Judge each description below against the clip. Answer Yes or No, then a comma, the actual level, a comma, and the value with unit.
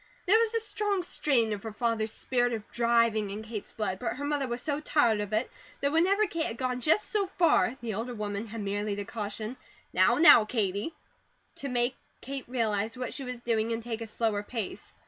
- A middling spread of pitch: Yes, average, 4.4 semitones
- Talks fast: Yes, fast, 210 wpm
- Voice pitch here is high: Yes, high, 235 Hz